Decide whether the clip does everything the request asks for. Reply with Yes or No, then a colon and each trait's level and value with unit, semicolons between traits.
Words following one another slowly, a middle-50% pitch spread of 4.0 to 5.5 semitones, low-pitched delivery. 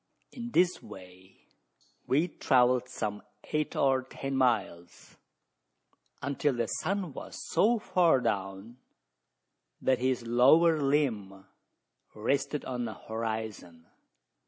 Yes: slow, 110 wpm; average, 5.2 semitones; low, 125 Hz